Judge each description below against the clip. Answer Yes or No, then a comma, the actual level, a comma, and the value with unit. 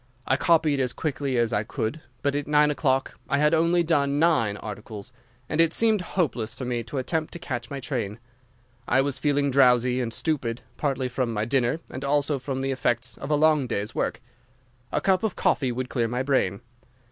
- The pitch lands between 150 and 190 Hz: No, low, 135 Hz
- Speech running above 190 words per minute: Yes, average, 200 wpm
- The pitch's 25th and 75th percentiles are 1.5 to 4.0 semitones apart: Yes, average, 3.6 semitones